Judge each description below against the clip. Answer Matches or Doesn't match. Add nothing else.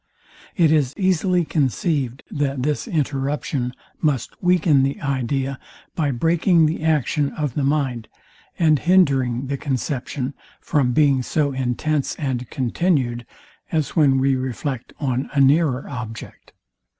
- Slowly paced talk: Matches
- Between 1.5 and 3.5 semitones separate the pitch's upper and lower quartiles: Matches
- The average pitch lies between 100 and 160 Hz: Matches